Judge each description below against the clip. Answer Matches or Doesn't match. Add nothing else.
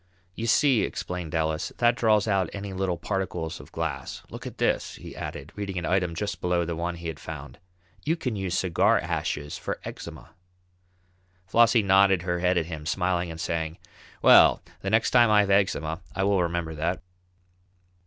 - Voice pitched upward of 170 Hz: Doesn't match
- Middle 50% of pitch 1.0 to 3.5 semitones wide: Matches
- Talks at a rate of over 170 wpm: Matches